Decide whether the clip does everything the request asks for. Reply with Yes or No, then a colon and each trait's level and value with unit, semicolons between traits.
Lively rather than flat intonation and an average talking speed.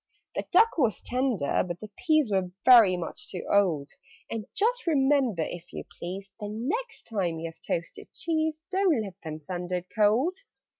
Yes: wide, 8.7 semitones; average, 170 wpm